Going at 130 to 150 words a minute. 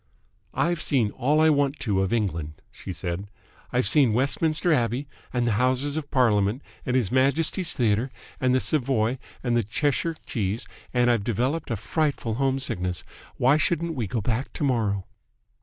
No: average, 170 wpm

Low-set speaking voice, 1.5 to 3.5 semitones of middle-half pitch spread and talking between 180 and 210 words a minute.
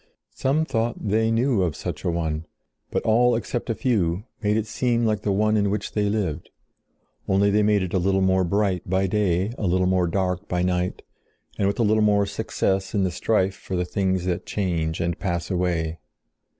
Yes: very low, 95 Hz; average, 3.0 semitones; average, 200 wpm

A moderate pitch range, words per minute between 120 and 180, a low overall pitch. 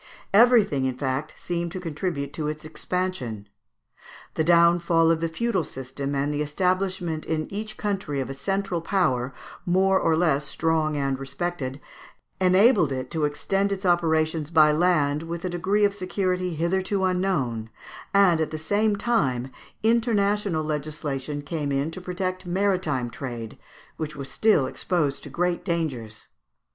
No: average, 4.4 semitones; average, 150 wpm; medium, 165 Hz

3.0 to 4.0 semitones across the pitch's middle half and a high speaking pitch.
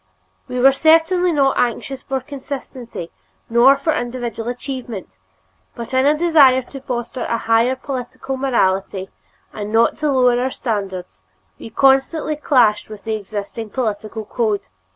Yes: average, 3.5 semitones; very high, 250 Hz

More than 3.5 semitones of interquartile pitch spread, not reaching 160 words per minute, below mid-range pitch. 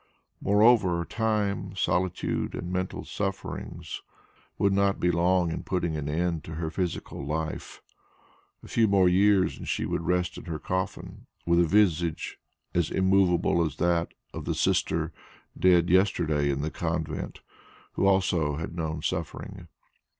No: average, 2.8 semitones; average, 145 wpm; very low, 90 Hz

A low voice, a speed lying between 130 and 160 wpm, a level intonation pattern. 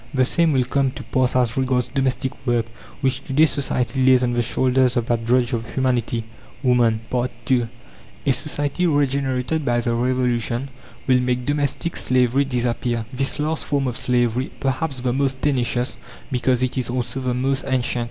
No: low, 130 Hz; average, 170 wpm; narrow, 1.8 semitones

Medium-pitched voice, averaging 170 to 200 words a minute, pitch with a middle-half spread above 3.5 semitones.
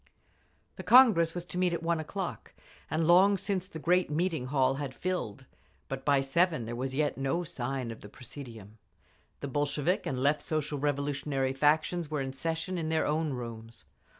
Yes: medium, 150 Hz; average, 180 wpm; average, 4.2 semitones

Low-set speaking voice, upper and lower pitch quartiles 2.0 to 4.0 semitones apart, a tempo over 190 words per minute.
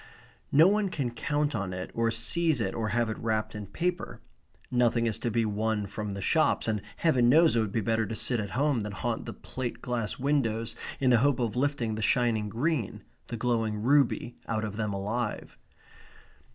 Yes: low, 115 Hz; average, 3.3 semitones; average, 200 wpm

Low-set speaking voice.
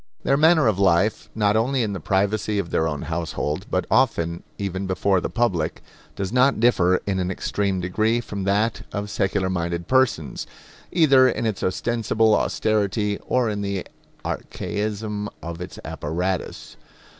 Yes: low, 100 Hz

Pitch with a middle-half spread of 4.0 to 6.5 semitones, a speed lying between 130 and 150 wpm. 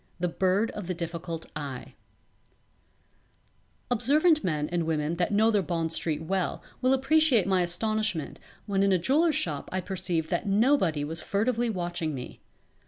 No: average, 5.1 semitones; average, 160 wpm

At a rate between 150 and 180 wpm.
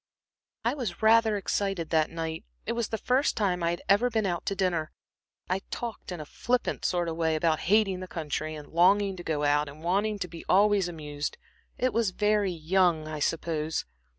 No: average, 200 wpm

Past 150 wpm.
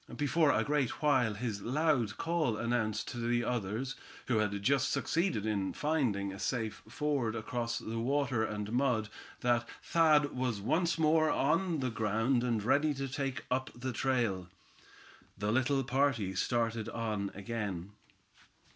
No: average, 145 wpm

